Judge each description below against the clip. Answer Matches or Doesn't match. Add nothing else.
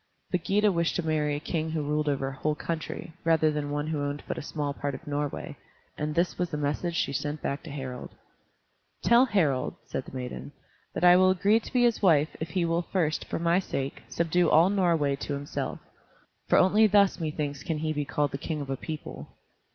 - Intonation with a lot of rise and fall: Doesn't match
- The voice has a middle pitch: Matches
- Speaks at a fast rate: Matches